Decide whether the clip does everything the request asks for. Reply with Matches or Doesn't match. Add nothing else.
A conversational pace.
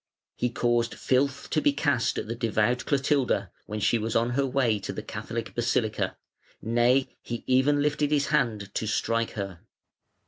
Matches